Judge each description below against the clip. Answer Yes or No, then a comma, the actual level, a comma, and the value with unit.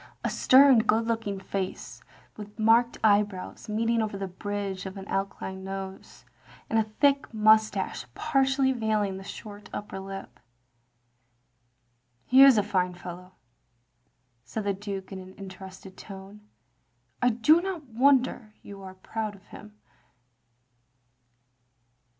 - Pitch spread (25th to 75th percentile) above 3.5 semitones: No, average, 2.9 semitones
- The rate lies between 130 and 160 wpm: Yes, slow, 135 wpm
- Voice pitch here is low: No, high, 205 Hz